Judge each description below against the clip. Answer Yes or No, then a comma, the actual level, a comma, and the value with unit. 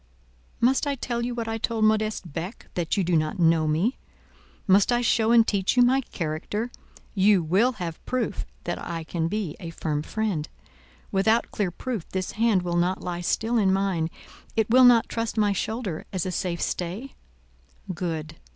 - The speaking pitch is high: Yes, high, 195 Hz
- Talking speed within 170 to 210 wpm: Yes, average, 180 wpm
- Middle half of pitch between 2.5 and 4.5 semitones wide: No, average, 4.9 semitones